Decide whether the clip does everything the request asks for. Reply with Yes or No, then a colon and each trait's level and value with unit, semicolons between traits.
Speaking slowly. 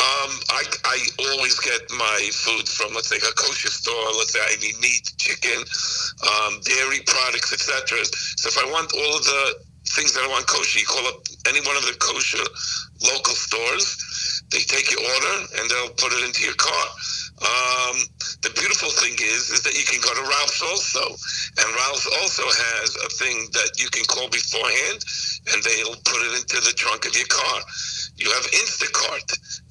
No: average, 190 wpm